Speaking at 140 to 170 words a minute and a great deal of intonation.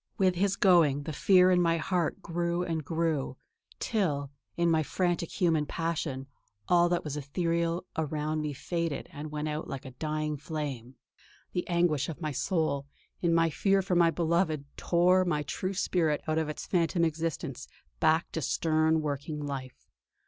No: average, 165 wpm; narrow, 2.6 semitones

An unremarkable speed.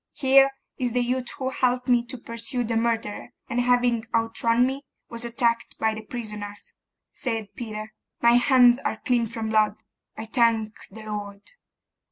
Yes: average, 160 wpm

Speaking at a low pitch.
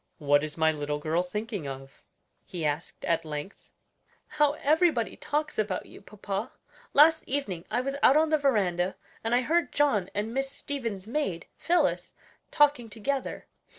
No: high, 220 Hz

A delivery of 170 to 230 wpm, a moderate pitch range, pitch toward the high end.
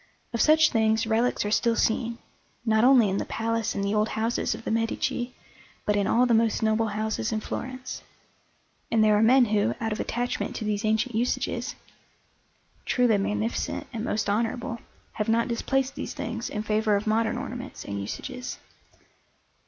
No: average, 175 wpm; narrow, 1.9 semitones; high, 225 Hz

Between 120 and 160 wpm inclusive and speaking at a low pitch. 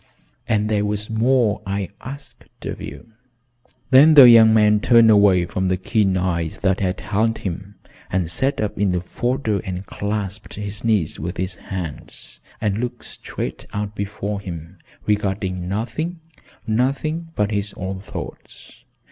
Yes: average, 150 wpm; low, 105 Hz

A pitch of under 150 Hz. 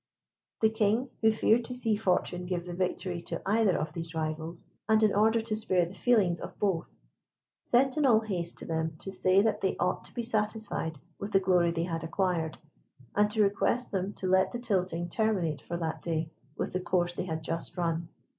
No: medium, 185 Hz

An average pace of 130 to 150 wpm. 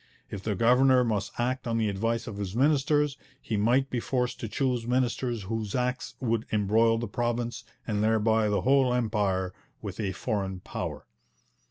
No: average, 170 wpm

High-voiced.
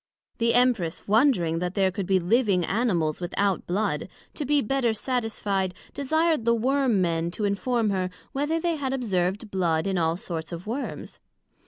Yes: high, 205 Hz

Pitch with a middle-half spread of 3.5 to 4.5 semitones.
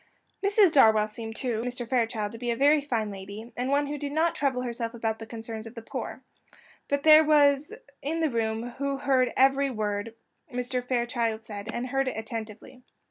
Yes: average, 3.8 semitones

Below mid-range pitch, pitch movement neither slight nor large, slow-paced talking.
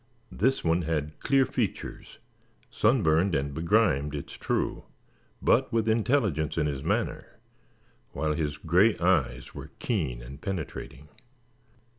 No: very low, 80 Hz; wide, 6.5 semitones; slow, 125 wpm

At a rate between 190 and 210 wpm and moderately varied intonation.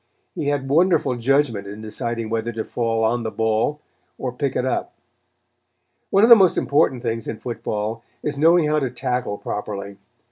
No: average, 175 wpm; average, 4.3 semitones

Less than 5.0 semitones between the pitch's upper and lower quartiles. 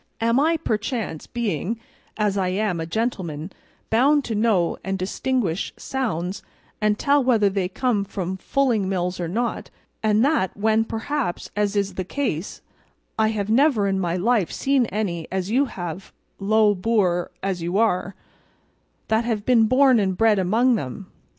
Yes: average, 3.9 semitones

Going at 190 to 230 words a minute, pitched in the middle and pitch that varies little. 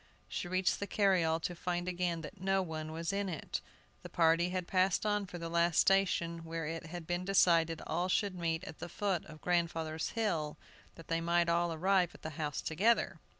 Yes: average, 200 wpm; medium, 175 Hz; narrow, 2.2 semitones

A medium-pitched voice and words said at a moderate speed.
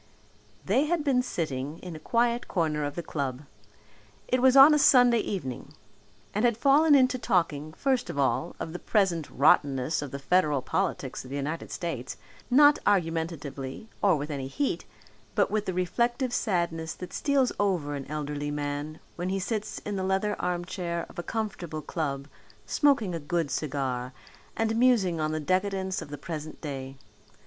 Yes: medium, 170 Hz; average, 170 wpm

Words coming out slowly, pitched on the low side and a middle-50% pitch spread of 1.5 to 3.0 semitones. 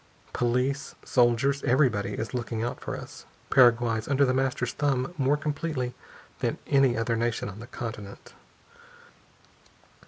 Yes: slow, 130 wpm; low, 125 Hz; average, 2.7 semitones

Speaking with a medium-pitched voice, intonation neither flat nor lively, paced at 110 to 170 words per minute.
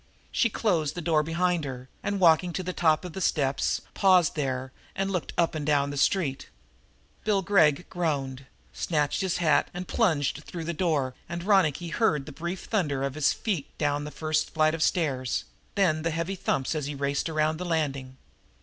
No: medium, 160 Hz; average, 3.7 semitones; average, 190 wpm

